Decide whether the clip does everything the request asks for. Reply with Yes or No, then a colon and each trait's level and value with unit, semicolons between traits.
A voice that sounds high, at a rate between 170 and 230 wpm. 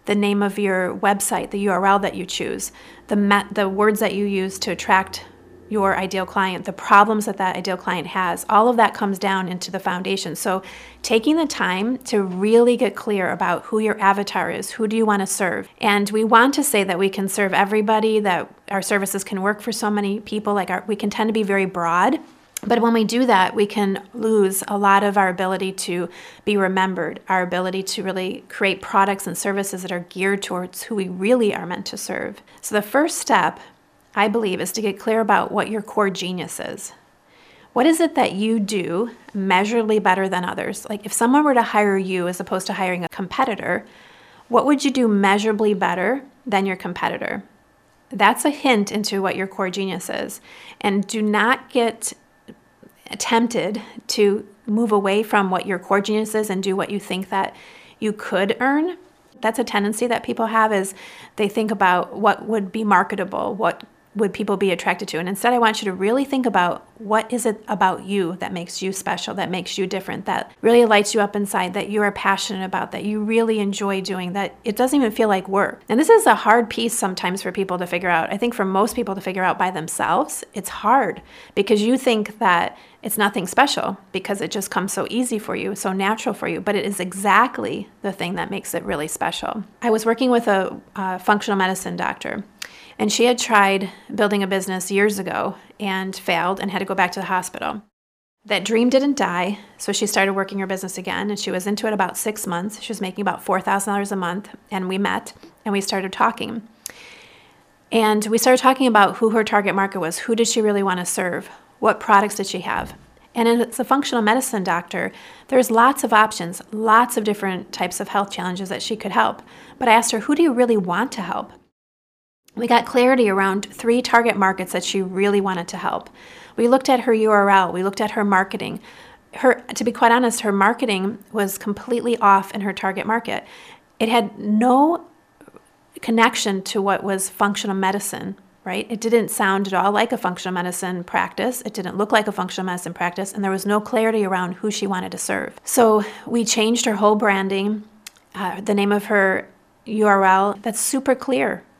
Yes: high, 205 Hz; fast, 205 wpm